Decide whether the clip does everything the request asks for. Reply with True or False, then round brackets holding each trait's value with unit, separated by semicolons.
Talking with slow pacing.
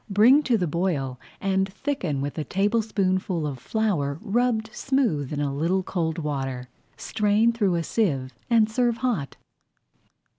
False (145 wpm)